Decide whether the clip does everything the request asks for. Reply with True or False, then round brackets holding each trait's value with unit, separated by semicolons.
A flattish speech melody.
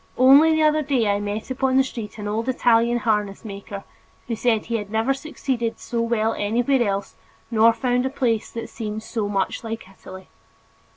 False (3.4 semitones)